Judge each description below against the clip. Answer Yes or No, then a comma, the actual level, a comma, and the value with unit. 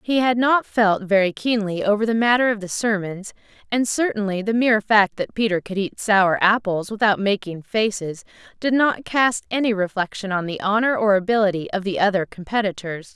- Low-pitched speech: No, high, 205 Hz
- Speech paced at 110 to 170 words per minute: No, average, 180 wpm